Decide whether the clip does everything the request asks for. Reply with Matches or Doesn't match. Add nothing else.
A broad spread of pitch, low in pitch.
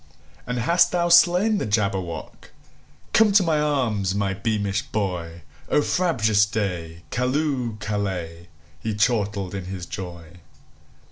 Matches